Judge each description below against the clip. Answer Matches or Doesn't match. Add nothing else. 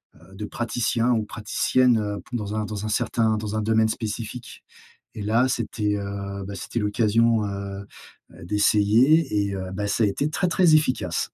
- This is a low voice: Matches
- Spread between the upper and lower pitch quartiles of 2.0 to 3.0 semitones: Matches